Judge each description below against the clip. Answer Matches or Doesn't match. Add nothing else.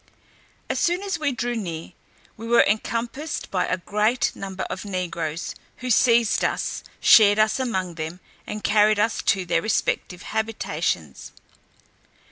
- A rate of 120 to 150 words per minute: Matches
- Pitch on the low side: Doesn't match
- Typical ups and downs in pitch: Matches